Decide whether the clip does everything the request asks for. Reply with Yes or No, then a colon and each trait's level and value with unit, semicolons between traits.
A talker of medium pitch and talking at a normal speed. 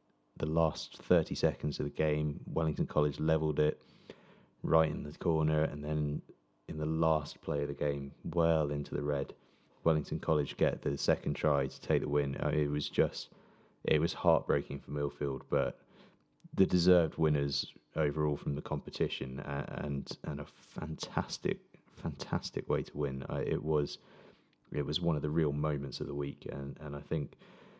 No: very low, 75 Hz; average, 170 wpm